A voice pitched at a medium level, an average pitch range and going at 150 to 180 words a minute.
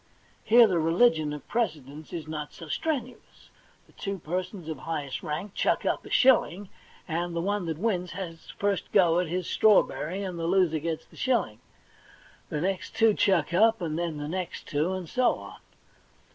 Yes: medium, 175 Hz; average, 3.9 semitones; average, 170 wpm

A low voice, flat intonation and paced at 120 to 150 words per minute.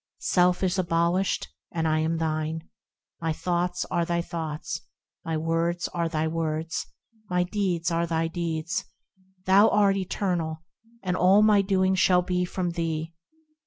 No: medium, 170 Hz; narrow, 1.9 semitones; average, 145 wpm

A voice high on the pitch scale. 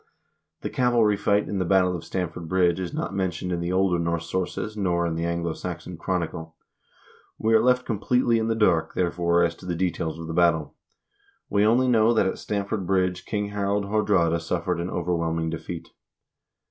No: very low, 90 Hz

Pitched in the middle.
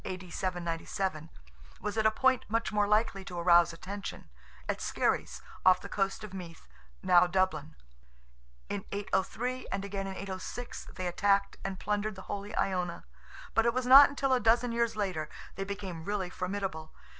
No: high, 195 Hz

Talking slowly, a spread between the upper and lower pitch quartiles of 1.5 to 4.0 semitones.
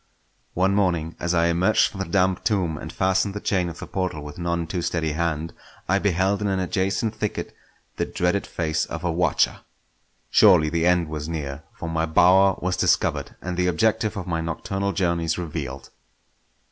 No: average, 185 wpm; average, 2.8 semitones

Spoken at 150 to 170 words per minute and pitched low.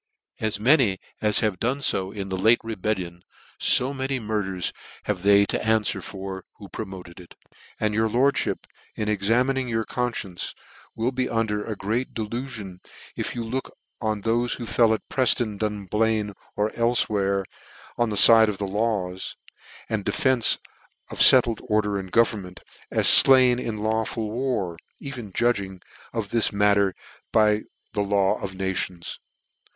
Yes: average, 155 wpm; low, 110 Hz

